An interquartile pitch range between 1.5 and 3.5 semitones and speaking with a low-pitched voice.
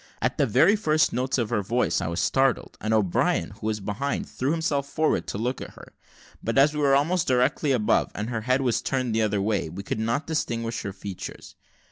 No: average, 4.6 semitones; low, 120 Hz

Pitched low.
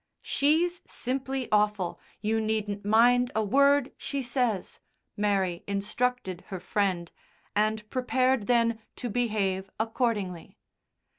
No: high, 220 Hz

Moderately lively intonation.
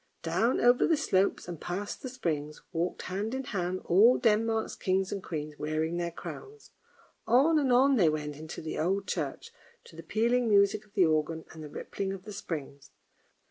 No: wide, 6.2 semitones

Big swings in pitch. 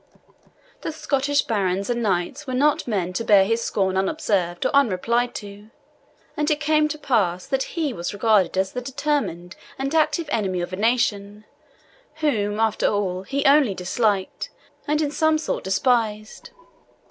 Yes: wide, 6.6 semitones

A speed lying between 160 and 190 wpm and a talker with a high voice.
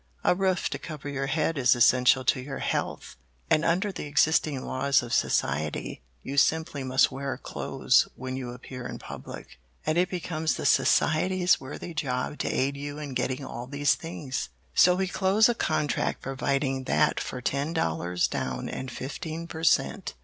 No: average, 170 wpm; medium, 140 Hz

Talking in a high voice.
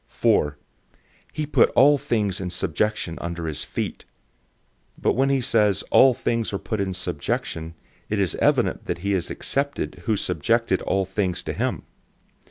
No: low, 100 Hz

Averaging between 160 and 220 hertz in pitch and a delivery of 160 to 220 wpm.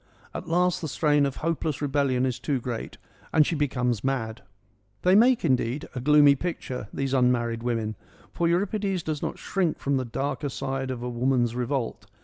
No: low, 135 Hz; average, 180 wpm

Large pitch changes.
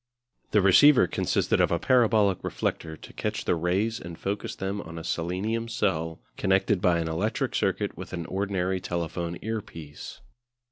No: average, 3.7 semitones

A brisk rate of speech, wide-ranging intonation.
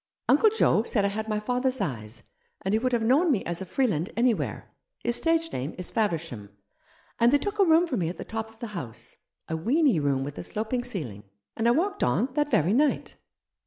Yes: fast, 235 wpm; wide, 7.7 semitones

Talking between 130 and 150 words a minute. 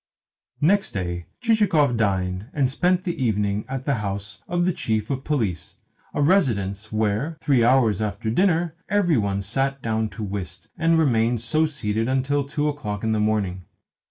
No: average, 165 wpm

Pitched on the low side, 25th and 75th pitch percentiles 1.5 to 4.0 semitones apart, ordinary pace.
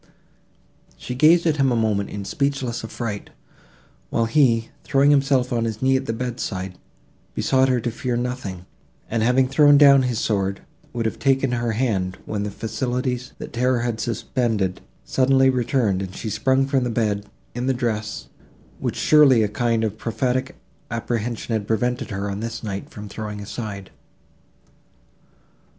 Yes: low, 120 Hz; average, 3.4 semitones; average, 165 wpm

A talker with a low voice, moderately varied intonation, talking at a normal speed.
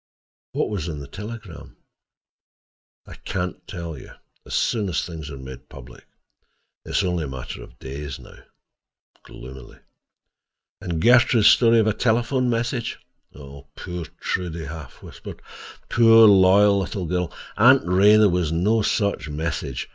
No: very low, 90 Hz; wide, 6.1 semitones; average, 145 wpm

